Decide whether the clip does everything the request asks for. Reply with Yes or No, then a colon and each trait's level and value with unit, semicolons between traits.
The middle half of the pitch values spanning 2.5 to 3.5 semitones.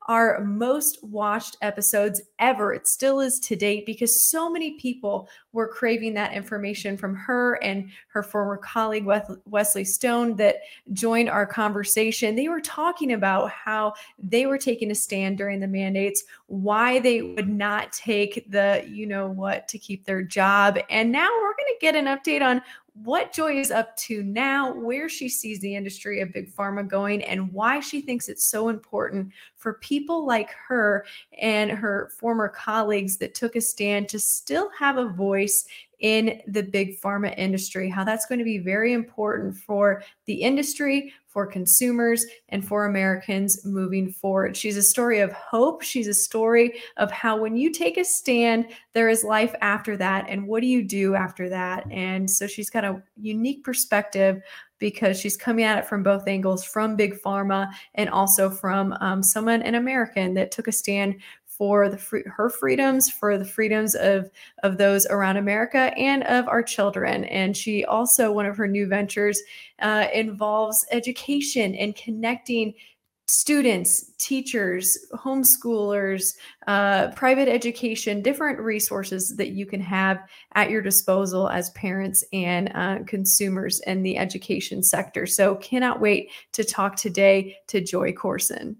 Yes: average, 3.0 semitones